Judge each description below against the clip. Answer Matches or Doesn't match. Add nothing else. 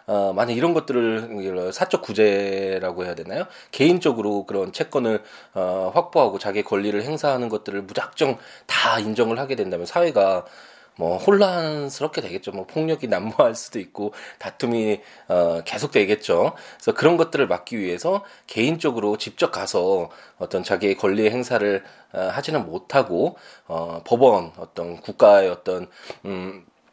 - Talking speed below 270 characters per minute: Doesn't match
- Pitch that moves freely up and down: Doesn't match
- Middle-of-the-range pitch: Doesn't match